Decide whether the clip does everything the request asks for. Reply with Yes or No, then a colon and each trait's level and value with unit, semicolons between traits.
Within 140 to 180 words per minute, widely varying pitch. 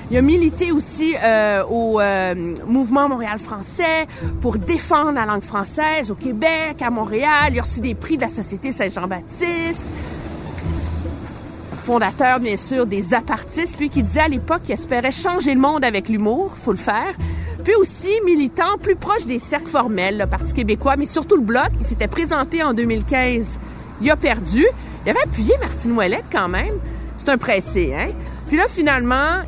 Yes: average, 175 wpm; wide, 6.9 semitones